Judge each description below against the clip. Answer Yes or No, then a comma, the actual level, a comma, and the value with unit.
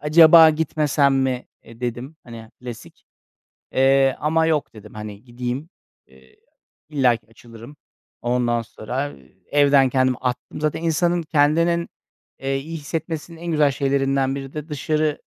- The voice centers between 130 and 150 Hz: Yes, medium, 140 Hz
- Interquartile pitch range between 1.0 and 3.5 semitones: No, average, 4.1 semitones